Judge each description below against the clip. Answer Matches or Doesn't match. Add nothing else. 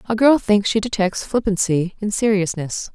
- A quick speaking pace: Doesn't match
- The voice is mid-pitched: Doesn't match